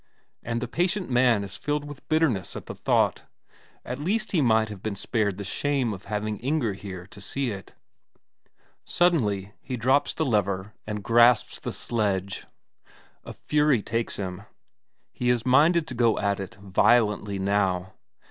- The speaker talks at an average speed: Yes, average, 160 wpm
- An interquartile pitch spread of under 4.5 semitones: No, average, 5.0 semitones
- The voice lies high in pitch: No, low, 110 Hz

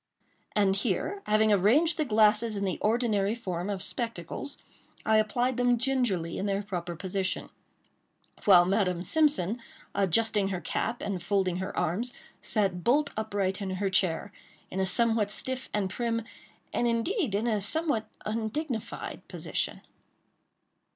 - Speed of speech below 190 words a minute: Yes, average, 140 wpm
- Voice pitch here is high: Yes, high, 210 Hz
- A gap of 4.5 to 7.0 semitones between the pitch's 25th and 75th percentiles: No, average, 3.7 semitones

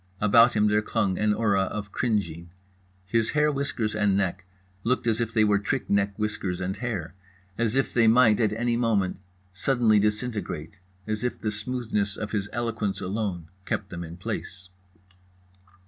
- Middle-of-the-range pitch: No, low, 105 Hz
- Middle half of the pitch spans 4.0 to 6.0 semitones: No, average, 2.8 semitones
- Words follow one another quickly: No, average, 165 wpm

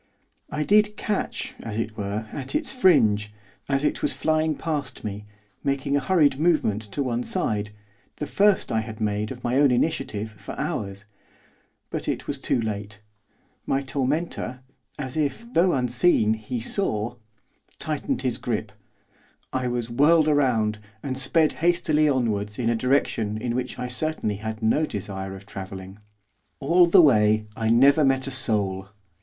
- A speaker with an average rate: Yes, average, 160 wpm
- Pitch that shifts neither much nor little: No, wide, 5.7 semitones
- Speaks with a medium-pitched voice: No, low, 125 Hz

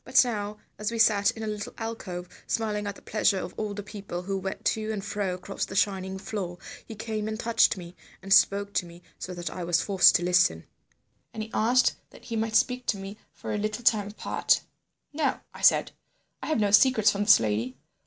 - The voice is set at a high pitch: Yes, high, 205 Hz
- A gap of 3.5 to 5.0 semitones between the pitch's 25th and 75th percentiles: No, narrow, 2.5 semitones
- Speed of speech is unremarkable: No, fast, 220 wpm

